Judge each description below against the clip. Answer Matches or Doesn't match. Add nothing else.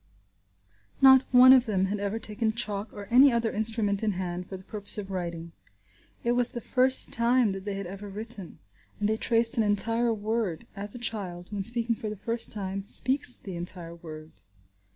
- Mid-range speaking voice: Doesn't match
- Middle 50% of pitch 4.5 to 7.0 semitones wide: Doesn't match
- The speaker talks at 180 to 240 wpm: Matches